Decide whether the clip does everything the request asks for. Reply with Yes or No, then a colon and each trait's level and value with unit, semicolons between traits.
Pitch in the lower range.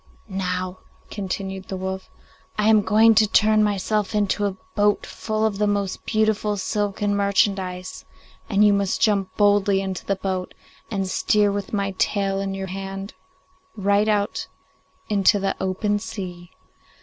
No: high, 200 Hz